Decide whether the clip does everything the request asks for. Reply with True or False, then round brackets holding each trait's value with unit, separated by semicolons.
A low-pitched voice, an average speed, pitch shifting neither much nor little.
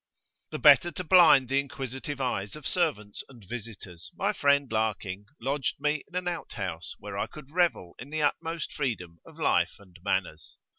False (130 Hz; 180 wpm; 6.9 semitones)